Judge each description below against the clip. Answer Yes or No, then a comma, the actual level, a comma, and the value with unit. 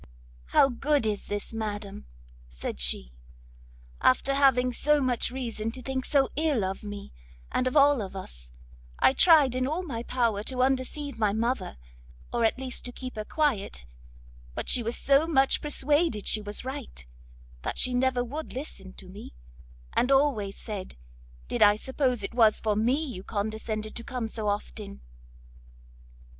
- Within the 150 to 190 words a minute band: Yes, average, 165 wpm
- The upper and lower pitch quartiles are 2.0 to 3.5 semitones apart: No, average, 4.5 semitones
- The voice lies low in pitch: No, high, 240 Hz